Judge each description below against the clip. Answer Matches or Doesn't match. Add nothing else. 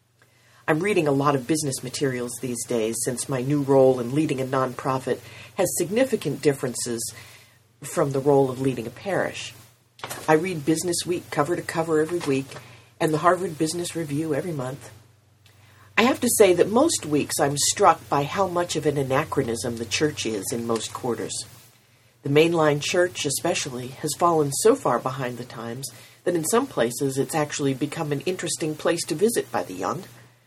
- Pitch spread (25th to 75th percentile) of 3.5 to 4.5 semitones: Doesn't match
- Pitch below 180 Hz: Matches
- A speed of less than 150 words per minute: Doesn't match